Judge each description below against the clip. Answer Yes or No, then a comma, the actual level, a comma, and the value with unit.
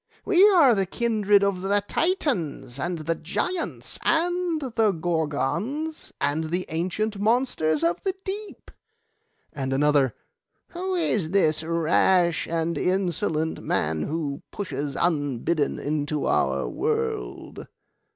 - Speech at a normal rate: No, slow, 115 wpm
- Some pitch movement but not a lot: No, wide, 8.4 semitones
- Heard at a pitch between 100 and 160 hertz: No, medium, 180 Hz